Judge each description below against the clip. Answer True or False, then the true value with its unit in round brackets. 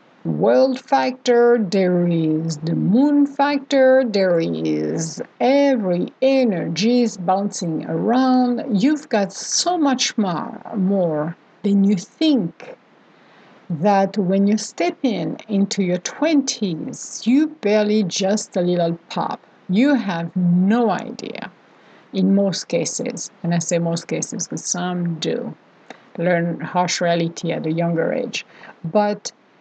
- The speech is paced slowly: True (120 wpm)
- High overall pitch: True (200 Hz)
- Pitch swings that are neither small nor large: False (6.4 semitones)